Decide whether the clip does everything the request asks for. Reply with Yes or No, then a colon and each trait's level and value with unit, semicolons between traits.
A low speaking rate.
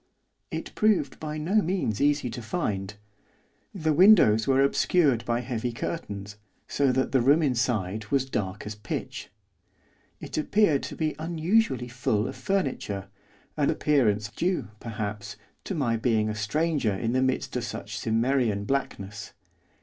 No: average, 145 wpm